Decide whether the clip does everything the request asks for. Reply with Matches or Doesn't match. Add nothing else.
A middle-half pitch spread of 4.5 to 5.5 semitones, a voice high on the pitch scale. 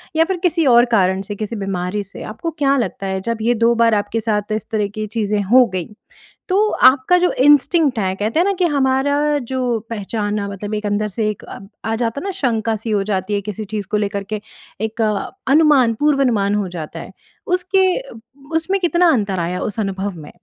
Matches